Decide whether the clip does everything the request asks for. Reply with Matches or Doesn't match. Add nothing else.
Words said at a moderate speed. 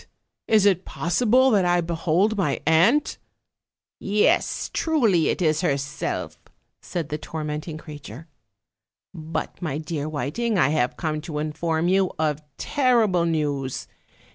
Doesn't match